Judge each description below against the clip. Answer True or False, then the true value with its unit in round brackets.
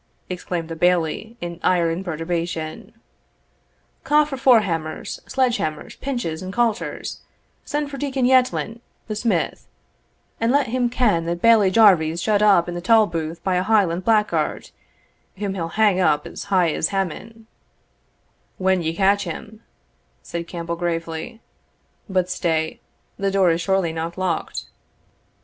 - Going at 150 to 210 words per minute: False (140 wpm)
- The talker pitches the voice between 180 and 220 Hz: True (185 Hz)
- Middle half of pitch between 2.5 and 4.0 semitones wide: False (4.9 semitones)